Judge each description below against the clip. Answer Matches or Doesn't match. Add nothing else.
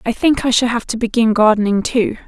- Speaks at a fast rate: Matches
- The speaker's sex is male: Doesn't match